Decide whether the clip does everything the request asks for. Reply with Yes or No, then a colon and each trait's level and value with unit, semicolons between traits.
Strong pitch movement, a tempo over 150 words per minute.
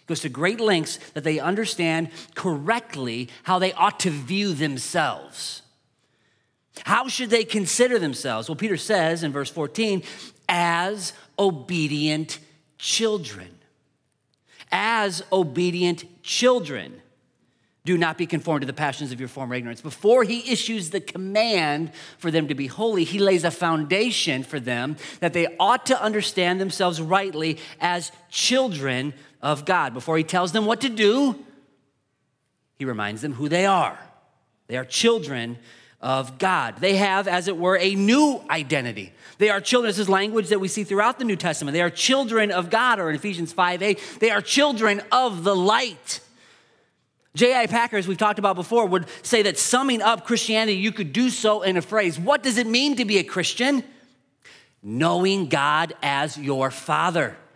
Yes: wide, 5.9 semitones; average, 165 wpm